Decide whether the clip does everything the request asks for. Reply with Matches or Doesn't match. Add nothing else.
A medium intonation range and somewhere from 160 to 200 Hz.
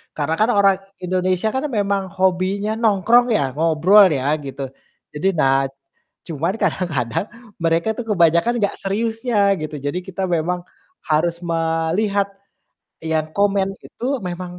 Matches